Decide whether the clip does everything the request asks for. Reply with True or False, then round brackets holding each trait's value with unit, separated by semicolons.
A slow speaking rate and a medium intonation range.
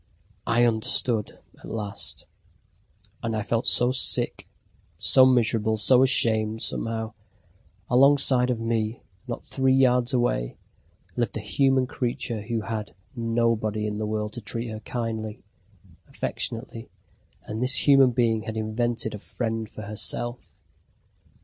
False (130 wpm; 2.2 semitones)